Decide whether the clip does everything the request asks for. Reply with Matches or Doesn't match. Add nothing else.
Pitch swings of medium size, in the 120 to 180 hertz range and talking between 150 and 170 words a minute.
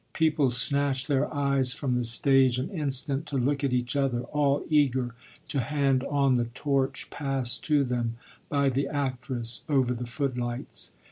Doesn't match